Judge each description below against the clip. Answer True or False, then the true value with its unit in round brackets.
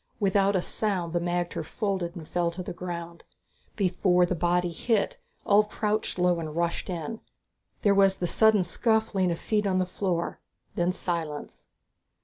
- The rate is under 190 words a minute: True (160 wpm)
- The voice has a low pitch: False (180 Hz)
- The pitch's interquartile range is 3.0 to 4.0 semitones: False (2.6 semitones)